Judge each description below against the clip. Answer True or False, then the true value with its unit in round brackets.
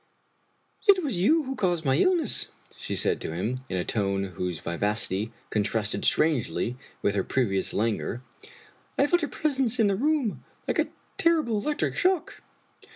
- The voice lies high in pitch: False (160 Hz)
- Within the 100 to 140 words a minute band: False (165 wpm)